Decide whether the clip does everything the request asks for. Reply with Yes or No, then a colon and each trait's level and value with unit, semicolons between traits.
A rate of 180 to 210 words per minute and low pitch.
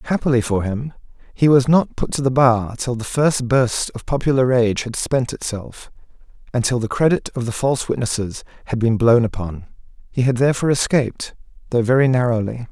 Yes: average, 185 wpm; low, 120 Hz